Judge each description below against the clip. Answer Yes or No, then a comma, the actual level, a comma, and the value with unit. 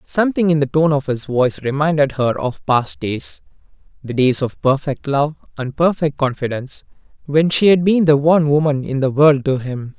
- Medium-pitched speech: Yes, medium, 145 Hz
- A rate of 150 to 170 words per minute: No, average, 185 wpm